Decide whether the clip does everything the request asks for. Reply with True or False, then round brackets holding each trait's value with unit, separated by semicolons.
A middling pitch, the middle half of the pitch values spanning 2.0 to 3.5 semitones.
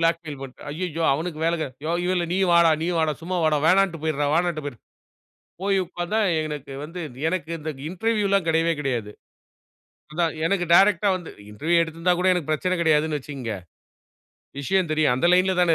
True (165 Hz; 2.8 semitones)